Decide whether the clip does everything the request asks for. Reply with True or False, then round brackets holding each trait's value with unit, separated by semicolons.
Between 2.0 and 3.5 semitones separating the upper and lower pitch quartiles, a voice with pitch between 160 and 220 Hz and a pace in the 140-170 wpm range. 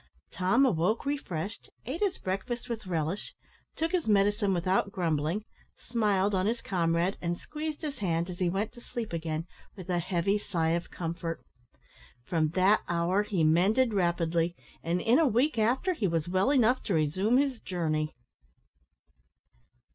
False (5.3 semitones; 190 Hz; 155 wpm)